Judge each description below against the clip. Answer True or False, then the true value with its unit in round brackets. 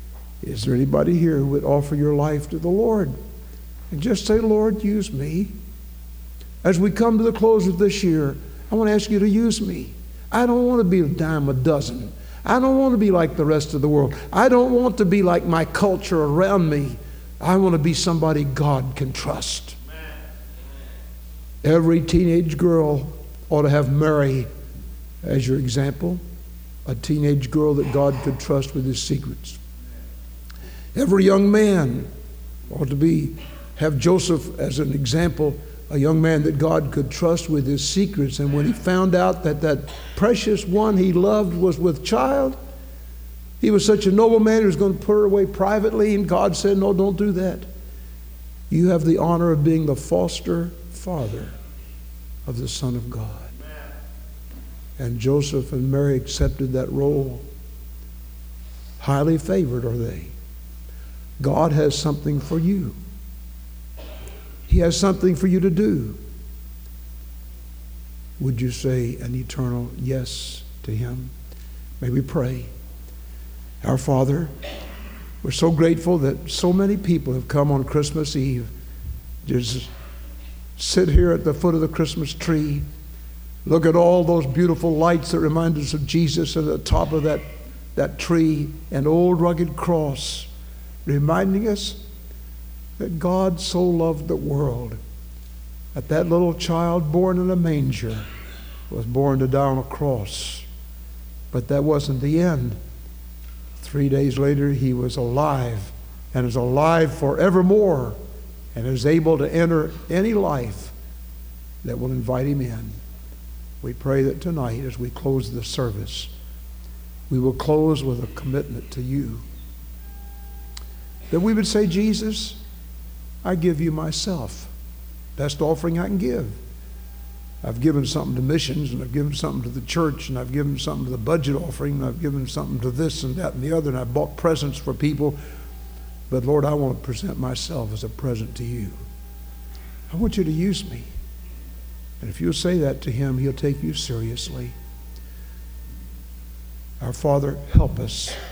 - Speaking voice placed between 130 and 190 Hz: True (135 Hz)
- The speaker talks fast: False (160 wpm)